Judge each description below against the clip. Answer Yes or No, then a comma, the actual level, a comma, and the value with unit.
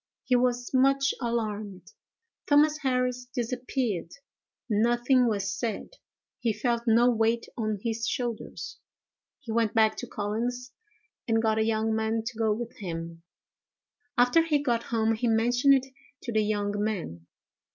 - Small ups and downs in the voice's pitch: Yes, narrow, 2.3 semitones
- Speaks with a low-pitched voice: No, high, 230 Hz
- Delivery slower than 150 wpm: Yes, average, 140 wpm